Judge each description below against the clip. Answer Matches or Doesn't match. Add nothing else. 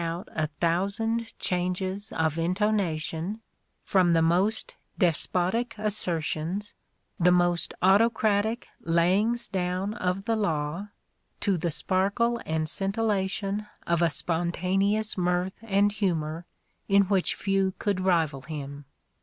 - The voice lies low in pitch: Doesn't match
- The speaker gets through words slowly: Matches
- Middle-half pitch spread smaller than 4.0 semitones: Matches